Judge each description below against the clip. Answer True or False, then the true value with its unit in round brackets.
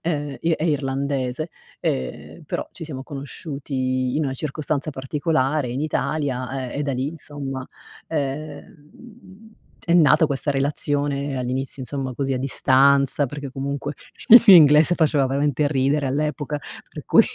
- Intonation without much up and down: True (2.2 semitones)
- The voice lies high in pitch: False (140 Hz)